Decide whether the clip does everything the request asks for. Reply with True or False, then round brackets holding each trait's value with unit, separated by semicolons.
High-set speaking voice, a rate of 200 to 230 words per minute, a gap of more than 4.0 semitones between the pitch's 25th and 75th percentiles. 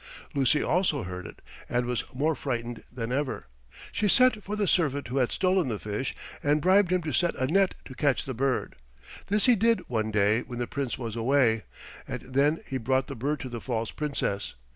False (135 Hz; 205 wpm; 5.2 semitones)